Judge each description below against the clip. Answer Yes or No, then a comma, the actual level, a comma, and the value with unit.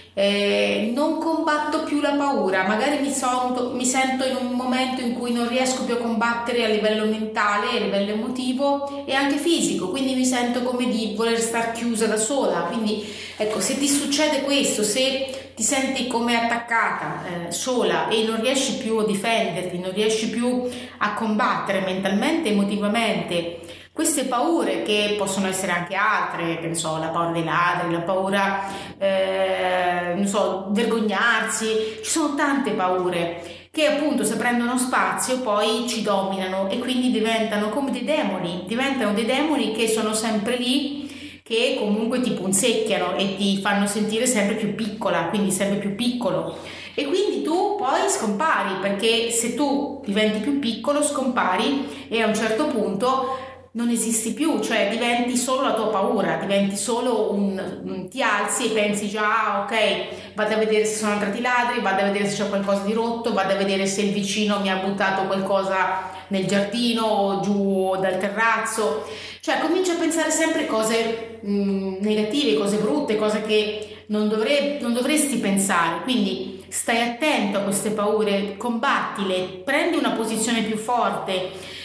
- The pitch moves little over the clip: No, average, 4.0 semitones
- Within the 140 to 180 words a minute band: Yes, average, 165 wpm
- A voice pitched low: No, high, 220 Hz